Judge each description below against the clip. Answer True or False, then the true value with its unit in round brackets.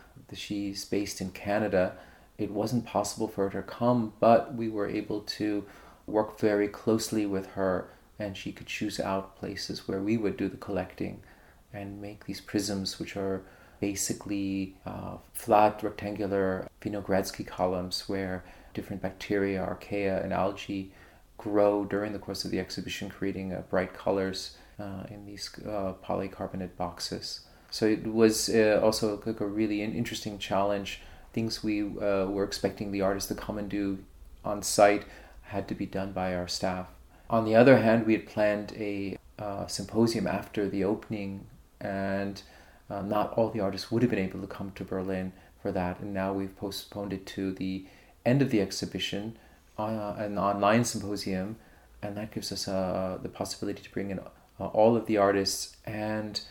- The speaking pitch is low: True (100 Hz)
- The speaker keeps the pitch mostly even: True (1.8 semitones)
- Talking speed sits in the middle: True (165 wpm)